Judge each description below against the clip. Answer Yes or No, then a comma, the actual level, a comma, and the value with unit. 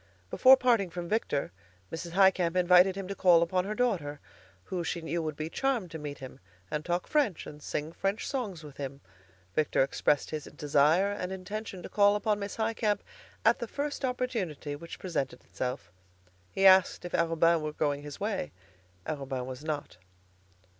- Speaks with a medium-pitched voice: Yes, medium, 175 Hz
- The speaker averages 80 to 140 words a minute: No, average, 175 wpm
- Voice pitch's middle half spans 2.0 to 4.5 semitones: No, average, 5.1 semitones